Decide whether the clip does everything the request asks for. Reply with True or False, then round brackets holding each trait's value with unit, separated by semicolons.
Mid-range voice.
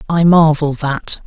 True (155 Hz)